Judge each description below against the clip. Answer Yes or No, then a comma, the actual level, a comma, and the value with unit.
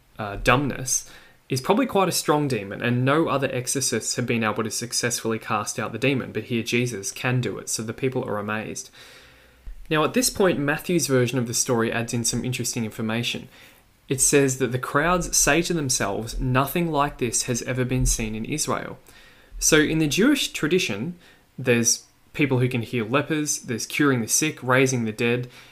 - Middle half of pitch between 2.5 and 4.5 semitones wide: Yes, average, 3.6 semitones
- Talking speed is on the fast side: No, average, 190 wpm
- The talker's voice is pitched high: No, low, 125 Hz